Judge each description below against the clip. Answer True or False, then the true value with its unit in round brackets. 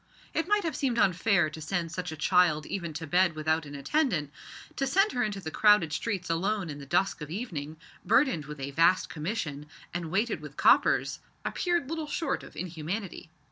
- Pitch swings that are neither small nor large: False (6.3 semitones)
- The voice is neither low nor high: True (180 Hz)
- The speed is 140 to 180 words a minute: False (190 wpm)